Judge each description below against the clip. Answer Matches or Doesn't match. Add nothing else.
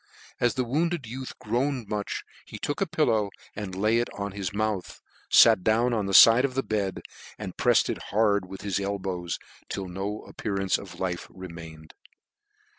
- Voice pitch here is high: Doesn't match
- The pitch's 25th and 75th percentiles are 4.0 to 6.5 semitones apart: Doesn't match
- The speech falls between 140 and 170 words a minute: Doesn't match